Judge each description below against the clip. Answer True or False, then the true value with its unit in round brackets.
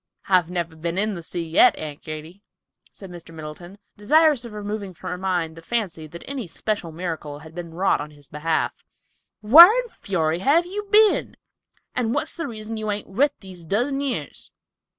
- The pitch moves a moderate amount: False (6.4 semitones)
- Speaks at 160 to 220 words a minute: True (185 wpm)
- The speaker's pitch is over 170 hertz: True (190 Hz)